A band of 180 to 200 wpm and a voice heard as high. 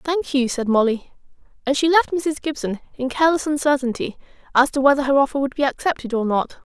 Yes: average, 195 wpm; very high, 280 Hz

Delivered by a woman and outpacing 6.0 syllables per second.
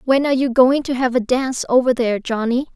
Yes: female; 6.3 syllables/s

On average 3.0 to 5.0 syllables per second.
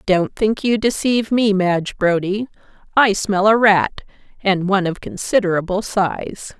Yes: 4.5 syllables/s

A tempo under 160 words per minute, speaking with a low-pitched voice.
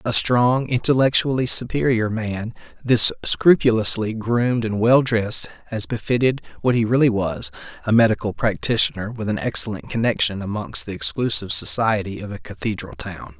Yes: average, 140 wpm; low, 110 Hz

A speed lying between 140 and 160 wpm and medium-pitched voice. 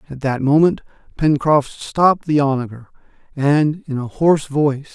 Yes: average, 145 wpm; medium, 145 Hz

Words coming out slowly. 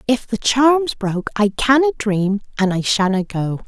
No: average, 180 wpm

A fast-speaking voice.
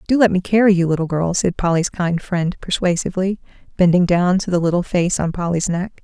Yes: fast, 210 wpm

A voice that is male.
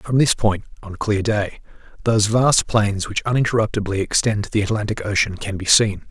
Yes: male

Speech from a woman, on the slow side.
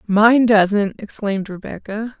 Yes: female; slow, 110 wpm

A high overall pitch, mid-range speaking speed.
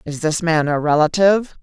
No: medium, 165 Hz; average, 185 wpm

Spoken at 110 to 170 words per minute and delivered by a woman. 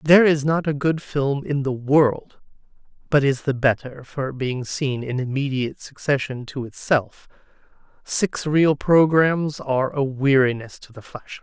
No: average, 160 wpm; male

